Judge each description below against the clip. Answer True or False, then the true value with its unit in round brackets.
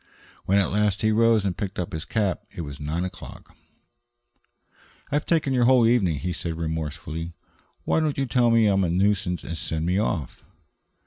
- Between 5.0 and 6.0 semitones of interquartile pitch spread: True (5.5 semitones)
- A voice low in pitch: True (95 Hz)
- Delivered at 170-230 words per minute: True (190 wpm)